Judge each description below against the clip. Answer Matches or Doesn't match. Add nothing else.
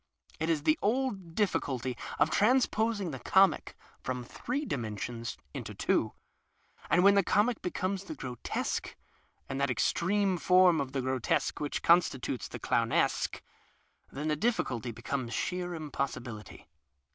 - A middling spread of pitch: Doesn't match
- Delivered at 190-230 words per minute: Doesn't match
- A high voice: Doesn't match